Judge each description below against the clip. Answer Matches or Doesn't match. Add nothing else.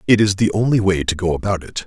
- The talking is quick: Matches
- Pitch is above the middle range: Doesn't match